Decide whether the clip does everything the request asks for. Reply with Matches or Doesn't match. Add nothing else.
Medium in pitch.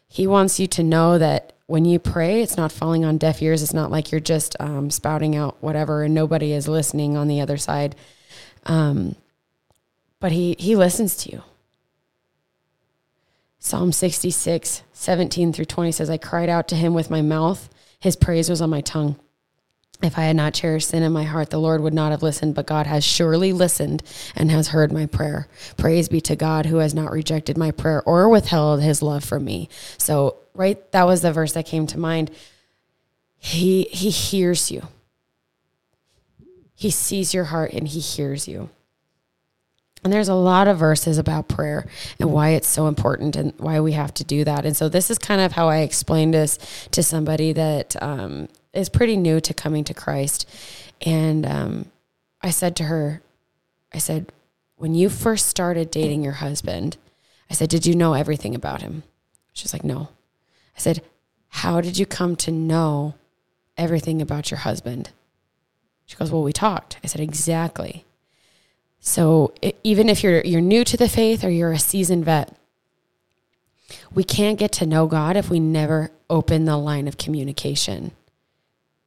Matches